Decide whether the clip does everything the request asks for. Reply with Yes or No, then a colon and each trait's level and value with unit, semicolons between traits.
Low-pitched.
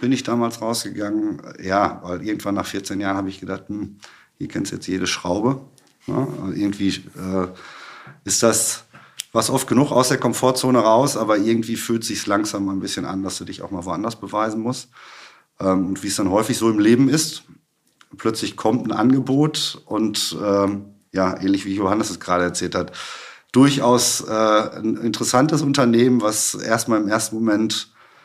Yes: low, 110 Hz